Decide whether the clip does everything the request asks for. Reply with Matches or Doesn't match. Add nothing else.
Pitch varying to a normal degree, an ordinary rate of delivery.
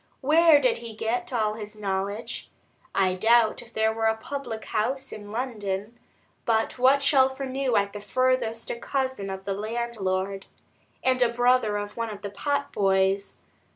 Matches